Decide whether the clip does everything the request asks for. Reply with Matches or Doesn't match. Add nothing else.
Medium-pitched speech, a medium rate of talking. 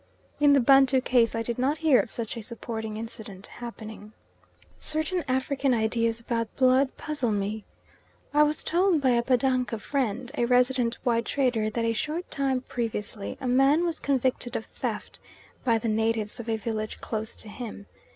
Doesn't match